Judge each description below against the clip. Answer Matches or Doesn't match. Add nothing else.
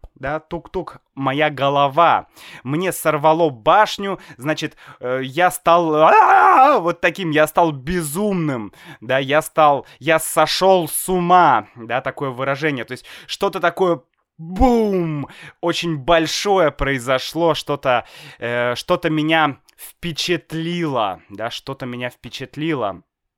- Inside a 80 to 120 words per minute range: Matches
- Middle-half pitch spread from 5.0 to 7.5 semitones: Doesn't match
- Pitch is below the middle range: Doesn't match